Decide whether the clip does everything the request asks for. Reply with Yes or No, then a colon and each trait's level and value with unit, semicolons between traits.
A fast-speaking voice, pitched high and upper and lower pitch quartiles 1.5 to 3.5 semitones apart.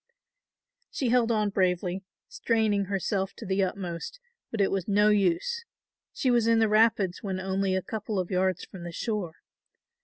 No: average, 165 wpm; high, 200 Hz; average, 2.9 semitones